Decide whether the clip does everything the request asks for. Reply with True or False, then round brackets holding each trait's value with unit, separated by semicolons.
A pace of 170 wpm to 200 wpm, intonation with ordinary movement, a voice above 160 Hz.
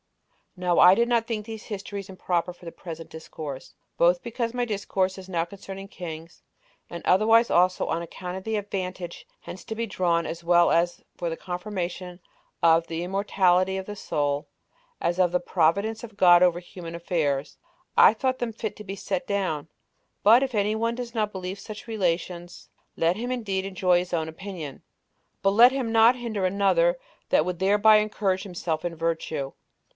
True (180 wpm; 3.6 semitones; 185 Hz)